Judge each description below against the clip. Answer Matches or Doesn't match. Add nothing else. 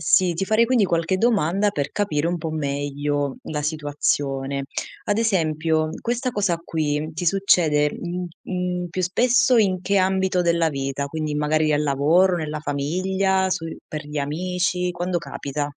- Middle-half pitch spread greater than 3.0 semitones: Matches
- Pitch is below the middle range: Doesn't match